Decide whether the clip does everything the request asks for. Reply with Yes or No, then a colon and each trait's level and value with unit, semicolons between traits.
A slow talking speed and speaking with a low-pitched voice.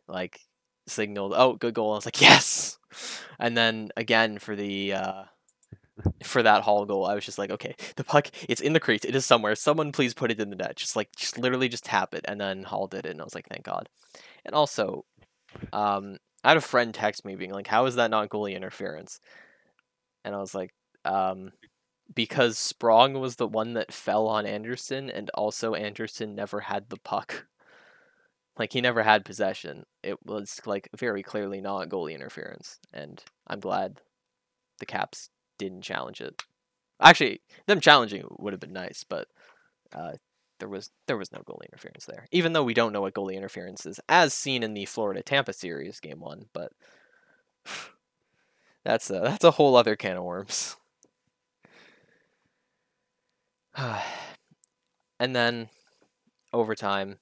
No: average, 175 wpm; low, 110 Hz